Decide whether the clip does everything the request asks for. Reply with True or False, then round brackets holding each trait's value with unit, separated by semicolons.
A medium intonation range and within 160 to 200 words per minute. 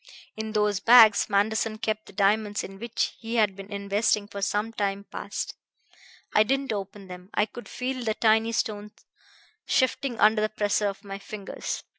False (1.8 semitones; 170 wpm)